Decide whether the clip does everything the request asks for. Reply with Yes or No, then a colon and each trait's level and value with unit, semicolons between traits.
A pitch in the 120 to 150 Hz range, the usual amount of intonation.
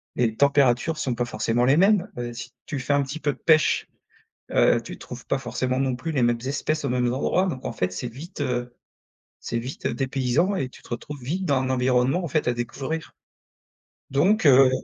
Yes: low, 130 Hz; average, 3.6 semitones